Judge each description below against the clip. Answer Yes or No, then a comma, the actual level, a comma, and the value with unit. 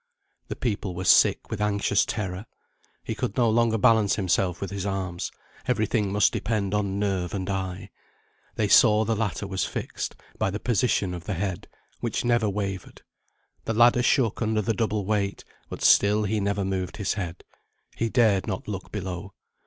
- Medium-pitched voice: No, low, 100 Hz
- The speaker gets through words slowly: No, average, 175 wpm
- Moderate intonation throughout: No, narrow, 2.3 semitones